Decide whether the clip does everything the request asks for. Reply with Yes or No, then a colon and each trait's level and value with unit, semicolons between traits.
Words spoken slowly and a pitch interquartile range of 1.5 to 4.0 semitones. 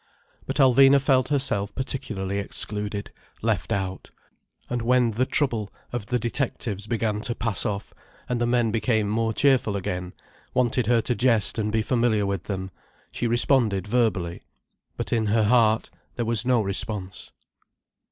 No: average, 150 wpm; average, 3.1 semitones